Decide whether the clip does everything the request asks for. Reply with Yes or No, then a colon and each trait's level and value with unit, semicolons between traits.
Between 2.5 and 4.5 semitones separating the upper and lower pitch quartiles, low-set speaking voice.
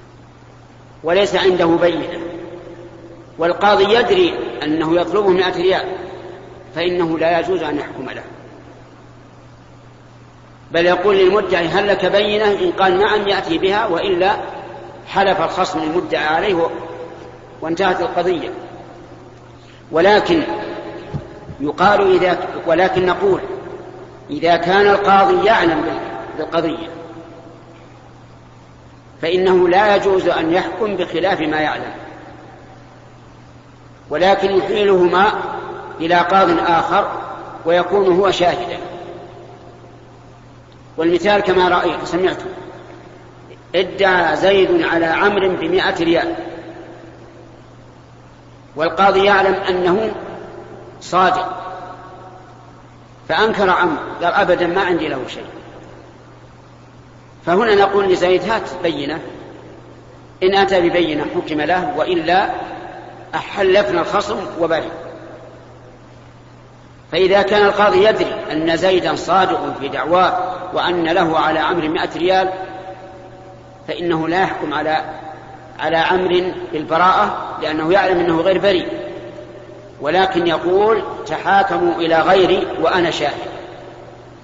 No: average, 2.9 semitones; medium, 180 Hz